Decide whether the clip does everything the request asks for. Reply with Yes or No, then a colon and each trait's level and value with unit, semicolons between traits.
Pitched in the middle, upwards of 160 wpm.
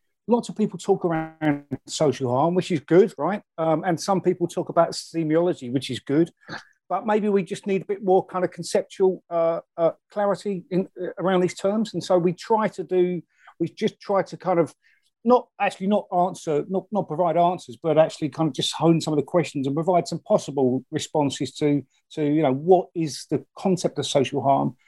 Yes: medium, 175 Hz; fast, 205 wpm